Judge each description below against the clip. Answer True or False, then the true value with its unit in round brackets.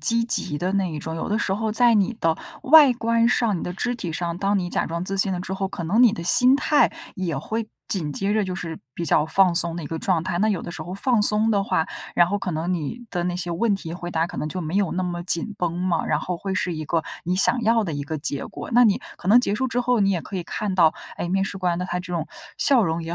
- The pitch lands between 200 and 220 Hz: False (185 Hz)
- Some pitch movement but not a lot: True (3.9 semitones)